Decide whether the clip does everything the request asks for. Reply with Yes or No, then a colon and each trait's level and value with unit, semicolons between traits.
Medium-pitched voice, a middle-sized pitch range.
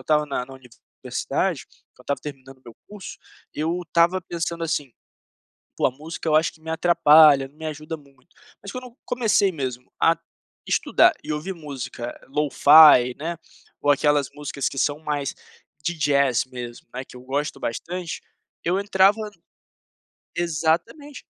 Yes: medium, 150 Hz; average, 3.7 semitones